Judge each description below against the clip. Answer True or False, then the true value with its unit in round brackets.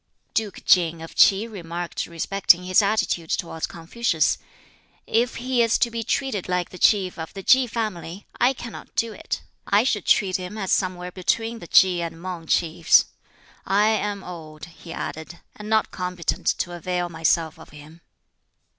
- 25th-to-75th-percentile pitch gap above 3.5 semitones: True (4.2 semitones)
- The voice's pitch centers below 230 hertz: True (185 Hz)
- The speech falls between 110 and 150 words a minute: False (165 wpm)